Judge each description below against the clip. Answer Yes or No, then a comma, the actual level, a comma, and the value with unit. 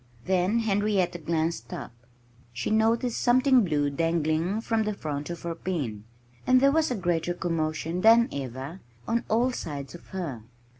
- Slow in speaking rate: No, average, 155 wpm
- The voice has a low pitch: No, medium, 175 Hz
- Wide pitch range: Yes, wide, 6.1 semitones